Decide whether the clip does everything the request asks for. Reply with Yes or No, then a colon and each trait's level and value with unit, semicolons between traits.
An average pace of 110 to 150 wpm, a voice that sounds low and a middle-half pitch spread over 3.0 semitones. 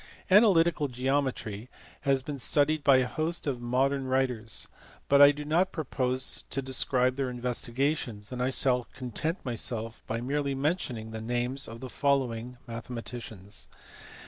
No: average, 145 wpm; low, 130 Hz; average, 2.7 semitones